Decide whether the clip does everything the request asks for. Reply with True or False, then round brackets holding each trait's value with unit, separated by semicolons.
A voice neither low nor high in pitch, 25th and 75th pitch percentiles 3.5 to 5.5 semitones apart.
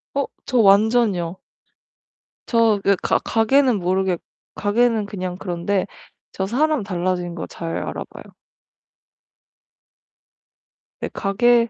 False (205 Hz; 4.2 semitones)